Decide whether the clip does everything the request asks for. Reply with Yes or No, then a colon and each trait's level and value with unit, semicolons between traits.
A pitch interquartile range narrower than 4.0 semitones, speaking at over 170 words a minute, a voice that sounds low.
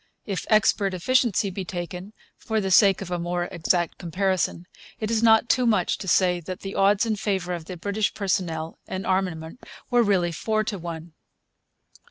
No: average, 3.1 semitones; average, 180 wpm; high, 190 Hz